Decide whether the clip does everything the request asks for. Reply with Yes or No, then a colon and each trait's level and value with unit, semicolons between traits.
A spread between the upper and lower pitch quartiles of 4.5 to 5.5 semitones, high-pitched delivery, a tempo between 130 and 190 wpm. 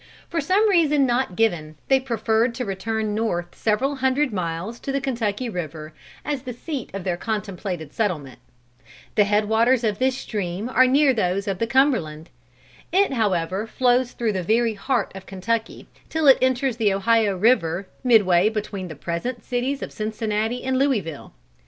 Yes: average, 5.2 semitones; high, 220 Hz; average, 165 wpm